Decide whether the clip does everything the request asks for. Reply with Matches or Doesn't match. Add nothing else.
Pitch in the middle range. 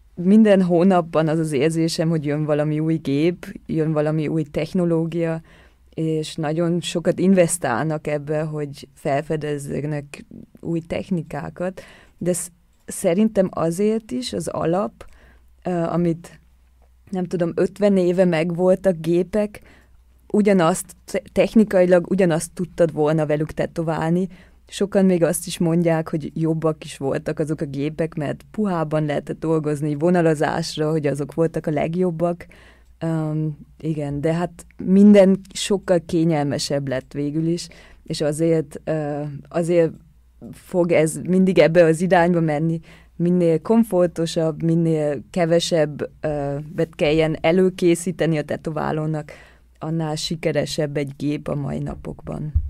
Matches